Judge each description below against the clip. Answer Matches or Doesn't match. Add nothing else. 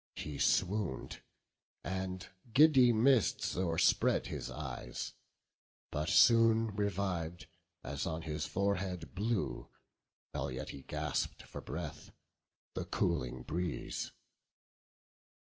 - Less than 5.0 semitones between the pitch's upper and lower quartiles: Doesn't match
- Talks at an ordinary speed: Doesn't match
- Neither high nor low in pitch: Doesn't match